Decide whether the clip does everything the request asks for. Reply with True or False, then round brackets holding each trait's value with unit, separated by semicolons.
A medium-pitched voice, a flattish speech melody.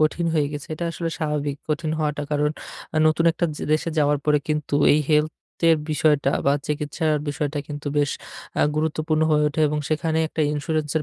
True (150 Hz; 1.1 semitones)